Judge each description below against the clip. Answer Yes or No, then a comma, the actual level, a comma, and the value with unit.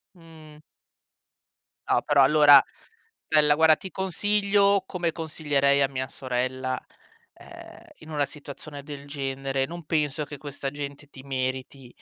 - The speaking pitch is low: No, medium, 145 Hz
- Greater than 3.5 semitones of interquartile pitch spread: No, narrow, 2.6 semitones